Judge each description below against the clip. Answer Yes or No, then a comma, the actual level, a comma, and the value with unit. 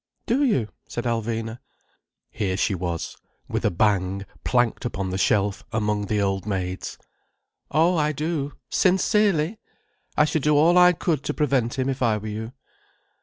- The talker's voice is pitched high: No, low, 120 Hz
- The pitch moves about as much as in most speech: No, wide, 6.8 semitones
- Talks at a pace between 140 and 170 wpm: Yes, average, 160 wpm